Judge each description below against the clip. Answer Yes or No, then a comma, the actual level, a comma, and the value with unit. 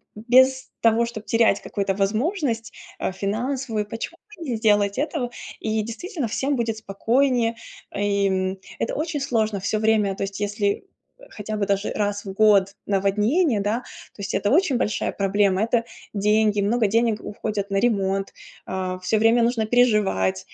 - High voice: Yes, high, 215 Hz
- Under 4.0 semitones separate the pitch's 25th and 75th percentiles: Yes, average, 2.9 semitones